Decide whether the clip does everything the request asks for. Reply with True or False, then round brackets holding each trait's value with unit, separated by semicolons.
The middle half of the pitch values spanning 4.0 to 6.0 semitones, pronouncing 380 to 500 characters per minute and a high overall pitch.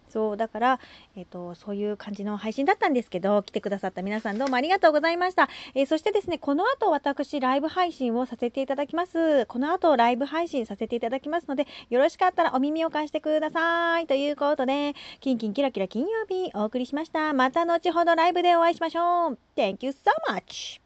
True (5.7 semitones; 480 characters per minute; 285 Hz)